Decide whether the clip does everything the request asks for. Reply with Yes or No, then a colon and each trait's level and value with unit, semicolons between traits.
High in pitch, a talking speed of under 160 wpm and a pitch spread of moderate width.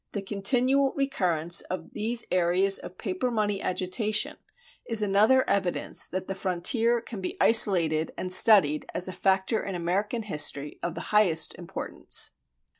Yes: high, 195 Hz; average, 145 wpm; average, 3.5 semitones